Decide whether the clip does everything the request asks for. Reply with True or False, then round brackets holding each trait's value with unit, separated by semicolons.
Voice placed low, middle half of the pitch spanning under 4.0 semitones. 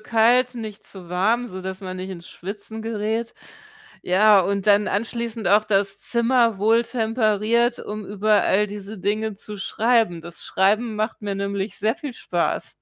False (215 Hz; 2.5 semitones)